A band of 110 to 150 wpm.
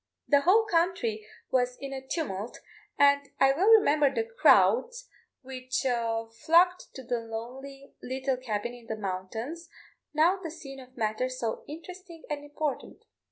Yes: average, 145 wpm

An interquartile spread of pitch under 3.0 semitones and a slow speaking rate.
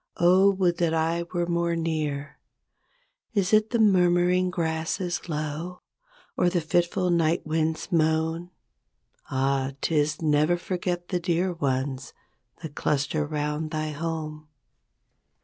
Yes: narrow, 2.4 semitones; slow, 120 wpm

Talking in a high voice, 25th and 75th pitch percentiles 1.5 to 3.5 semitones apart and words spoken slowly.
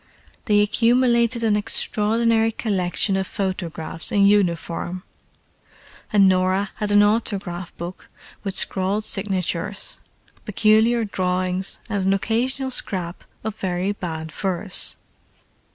Yes: high, 200 Hz; average, 2.9 semitones; slow, 105 wpm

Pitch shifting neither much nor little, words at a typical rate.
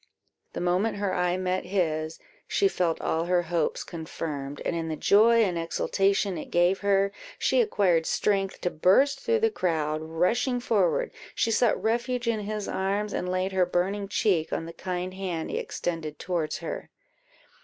Yes: average, 3.7 semitones; average, 170 wpm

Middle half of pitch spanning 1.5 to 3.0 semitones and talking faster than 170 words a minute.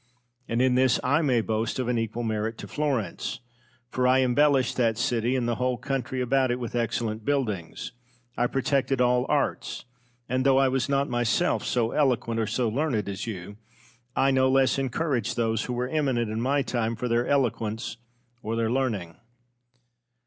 Yes: average, 2.7 semitones; average, 180 wpm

